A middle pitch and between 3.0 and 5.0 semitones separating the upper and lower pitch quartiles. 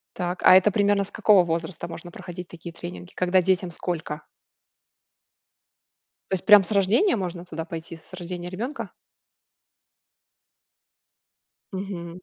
No: medium, 180 Hz; narrow, 2.4 semitones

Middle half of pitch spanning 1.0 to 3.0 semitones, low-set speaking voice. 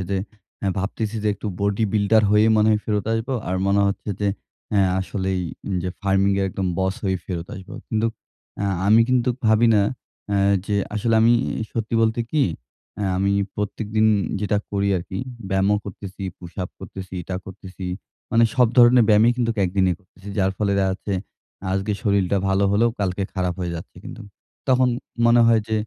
Yes: narrow, 2.5 semitones; low, 100 Hz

